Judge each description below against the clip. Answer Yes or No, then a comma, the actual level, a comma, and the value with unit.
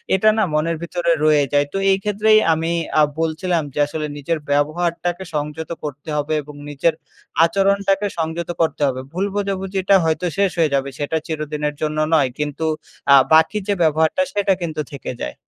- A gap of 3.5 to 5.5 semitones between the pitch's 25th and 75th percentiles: Yes, average, 4.0 semitones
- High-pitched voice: No, medium, 160 Hz